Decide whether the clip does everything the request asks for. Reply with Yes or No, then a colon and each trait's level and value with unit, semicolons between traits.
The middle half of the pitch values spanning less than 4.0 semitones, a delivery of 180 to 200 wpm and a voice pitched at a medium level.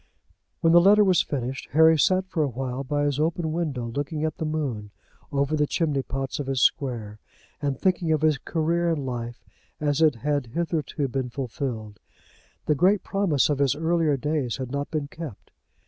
Yes: average, 3.4 semitones; average, 185 wpm; medium, 145 Hz